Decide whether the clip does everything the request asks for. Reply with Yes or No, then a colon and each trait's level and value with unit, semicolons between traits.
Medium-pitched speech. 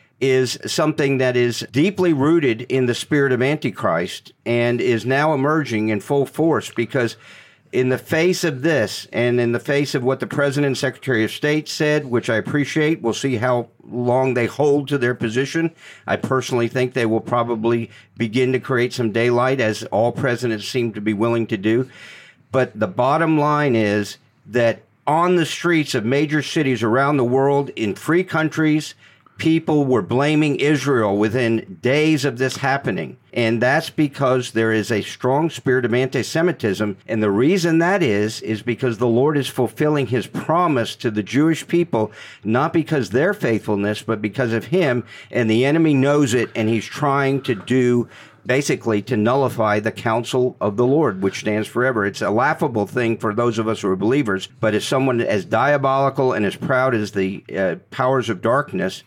No: low, 125 Hz